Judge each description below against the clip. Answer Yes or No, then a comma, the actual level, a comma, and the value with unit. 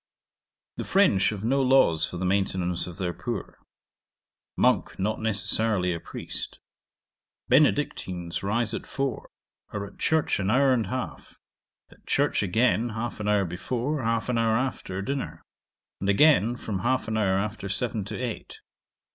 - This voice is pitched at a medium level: No, low, 110 Hz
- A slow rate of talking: No, average, 155 wpm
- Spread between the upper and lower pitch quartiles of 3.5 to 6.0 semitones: Yes, average, 4.3 semitones